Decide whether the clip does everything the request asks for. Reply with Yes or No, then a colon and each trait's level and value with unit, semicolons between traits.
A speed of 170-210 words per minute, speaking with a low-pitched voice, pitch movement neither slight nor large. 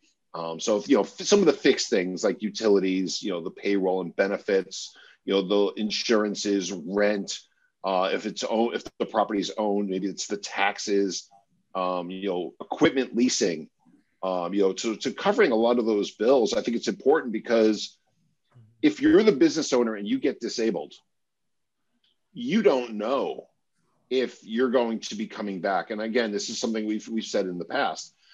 Yes: average, 185 wpm; low, 105 Hz; average, 3.9 semitones